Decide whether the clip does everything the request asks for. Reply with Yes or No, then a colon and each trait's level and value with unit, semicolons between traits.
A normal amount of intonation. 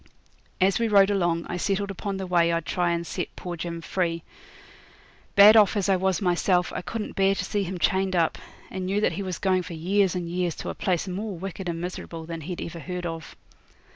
No: narrow, 2.3 semitones